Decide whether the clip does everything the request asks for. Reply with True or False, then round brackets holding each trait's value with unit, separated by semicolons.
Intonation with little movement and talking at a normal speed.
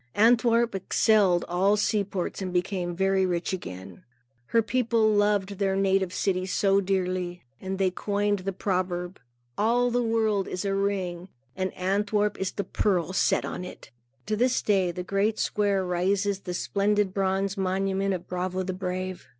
True (2.0 semitones; 160 wpm)